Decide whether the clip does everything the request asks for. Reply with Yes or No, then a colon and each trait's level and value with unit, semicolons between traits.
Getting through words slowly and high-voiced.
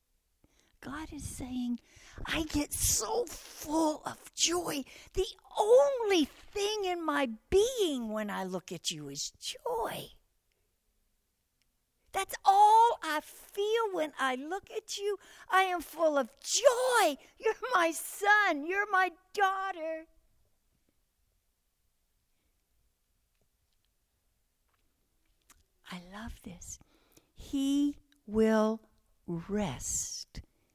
Yes: slow, 95 wpm; very high, 320 Hz